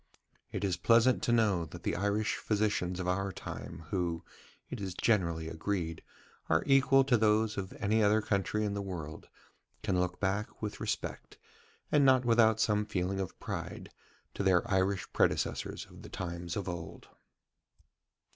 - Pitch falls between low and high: No, low, 100 Hz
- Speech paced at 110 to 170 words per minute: Yes, average, 160 wpm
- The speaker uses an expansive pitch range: No, average, 3.3 semitones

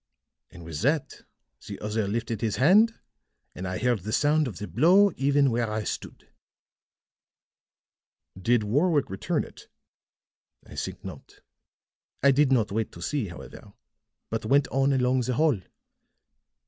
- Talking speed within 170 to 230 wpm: No, average, 145 wpm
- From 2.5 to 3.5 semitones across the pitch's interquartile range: No, average, 5.2 semitones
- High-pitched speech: No, low, 125 Hz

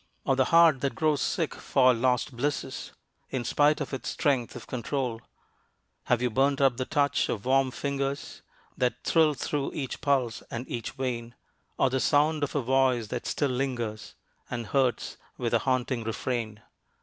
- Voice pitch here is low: Yes, low, 130 Hz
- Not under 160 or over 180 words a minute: Yes, average, 170 wpm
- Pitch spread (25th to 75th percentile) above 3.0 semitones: No, narrow, 2.6 semitones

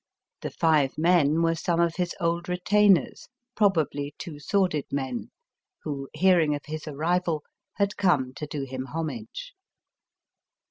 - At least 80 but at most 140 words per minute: Yes, slow, 135 wpm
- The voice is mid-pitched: Yes, medium, 165 Hz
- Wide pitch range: No, average, 3.5 semitones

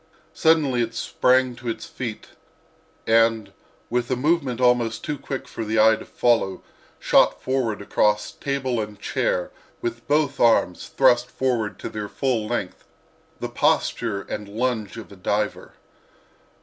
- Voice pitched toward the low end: Yes, low, 120 Hz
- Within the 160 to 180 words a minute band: No, average, 140 wpm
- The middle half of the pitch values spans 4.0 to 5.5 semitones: No, average, 3.3 semitones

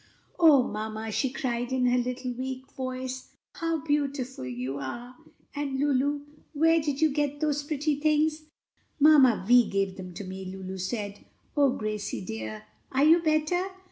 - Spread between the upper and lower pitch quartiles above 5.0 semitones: Yes, wide, 5.5 semitones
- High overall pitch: Yes, very high, 260 Hz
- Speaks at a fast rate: No, average, 155 wpm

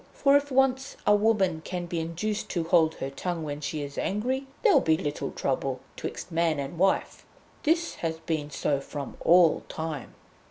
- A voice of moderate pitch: Yes, medium, 165 Hz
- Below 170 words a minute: No, average, 175 wpm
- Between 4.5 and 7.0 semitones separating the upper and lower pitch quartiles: Yes, wide, 5.6 semitones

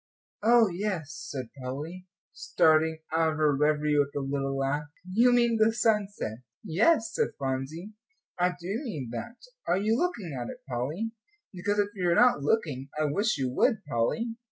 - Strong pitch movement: Yes, wide, 7.3 semitones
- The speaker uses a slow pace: No, average, 170 wpm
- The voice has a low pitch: No, medium, 165 Hz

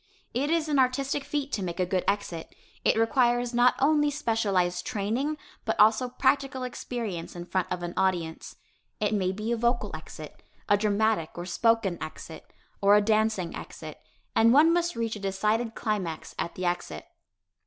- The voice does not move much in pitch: No, average, 5.1 semitones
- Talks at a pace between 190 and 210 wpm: No, average, 170 wpm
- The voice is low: No, high, 220 Hz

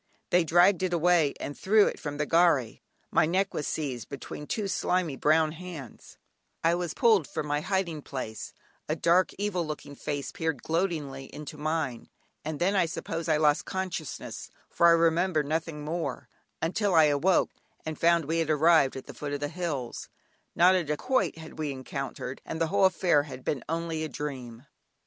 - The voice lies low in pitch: No, medium, 160 Hz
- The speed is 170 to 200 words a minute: Yes, average, 180 wpm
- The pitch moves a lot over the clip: No, average, 3.1 semitones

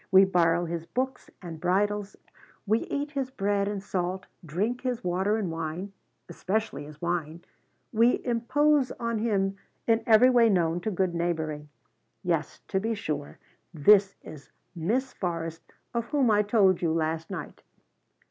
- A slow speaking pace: No, average, 150 wpm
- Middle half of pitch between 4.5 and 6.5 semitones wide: Yes, average, 5.0 semitones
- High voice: Yes, high, 195 Hz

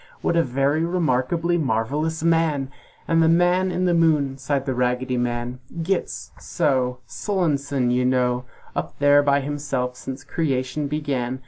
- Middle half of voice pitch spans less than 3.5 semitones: No, average, 4.3 semitones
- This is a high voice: No, medium, 140 Hz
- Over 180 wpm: No, average, 145 wpm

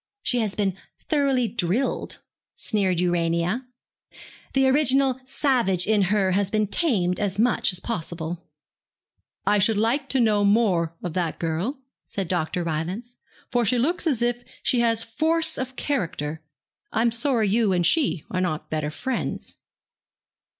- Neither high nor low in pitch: No, high, 215 Hz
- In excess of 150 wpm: No, average, 145 wpm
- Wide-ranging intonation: Yes, wide, 5.8 semitones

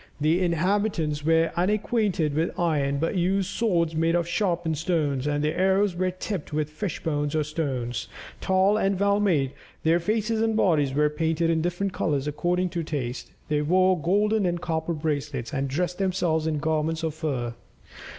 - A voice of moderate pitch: Yes, medium, 165 Hz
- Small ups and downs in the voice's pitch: No, average, 3.6 semitones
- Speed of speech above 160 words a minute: Yes, average, 170 wpm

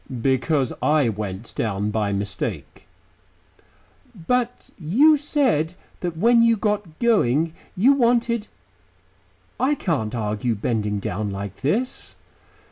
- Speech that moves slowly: Yes, slow, 110 wpm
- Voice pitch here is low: No, medium, 155 Hz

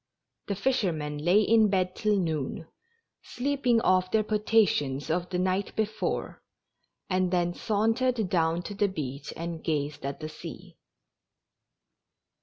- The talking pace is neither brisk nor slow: No, slow, 130 wpm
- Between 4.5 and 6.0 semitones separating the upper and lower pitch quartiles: Yes, average, 4.9 semitones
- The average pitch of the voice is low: No, medium, 185 Hz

